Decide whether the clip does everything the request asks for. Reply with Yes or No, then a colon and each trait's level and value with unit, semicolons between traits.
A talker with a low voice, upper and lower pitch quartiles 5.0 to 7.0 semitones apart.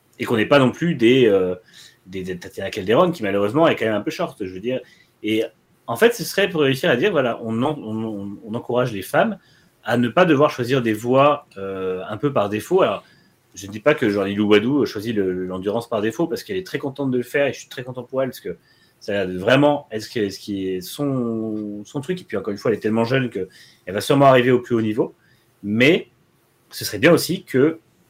Yes: low, 120 Hz; average, 5.3 semitones